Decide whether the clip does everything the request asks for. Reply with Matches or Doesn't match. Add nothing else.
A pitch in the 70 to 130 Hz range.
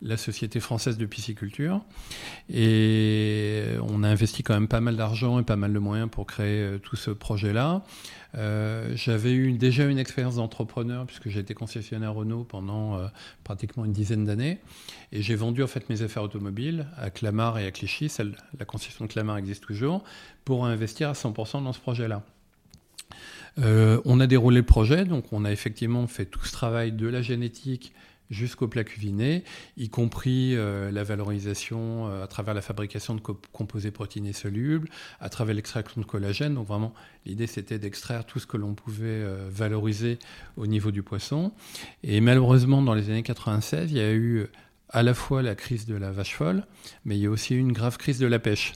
Matches